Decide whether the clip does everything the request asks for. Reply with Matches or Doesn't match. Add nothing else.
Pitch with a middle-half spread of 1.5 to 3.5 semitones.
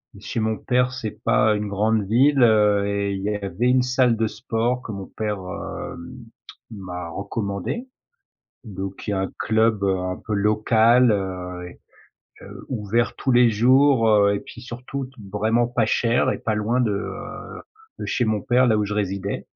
Matches